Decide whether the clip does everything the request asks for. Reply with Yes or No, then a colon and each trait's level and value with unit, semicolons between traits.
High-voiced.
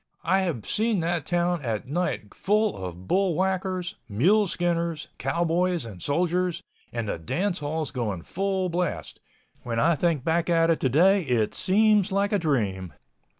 No: medium, 170 Hz